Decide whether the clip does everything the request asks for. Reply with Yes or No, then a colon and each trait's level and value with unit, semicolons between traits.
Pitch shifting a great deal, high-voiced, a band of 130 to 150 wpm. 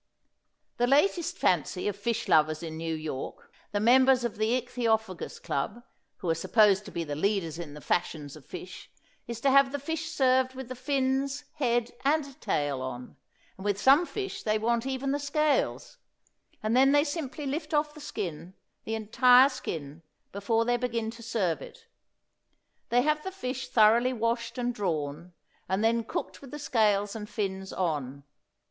No: wide, 6.2 semitones; high, 230 Hz; average, 175 wpm